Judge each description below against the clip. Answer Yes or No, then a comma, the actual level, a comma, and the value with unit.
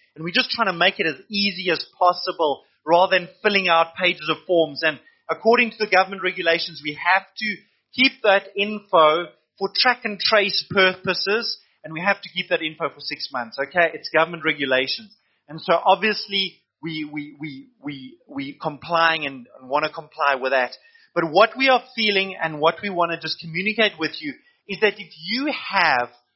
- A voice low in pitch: No, medium, 180 Hz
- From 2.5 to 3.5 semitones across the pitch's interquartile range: No, average, 4.5 semitones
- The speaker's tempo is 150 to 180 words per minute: No, average, 190 wpm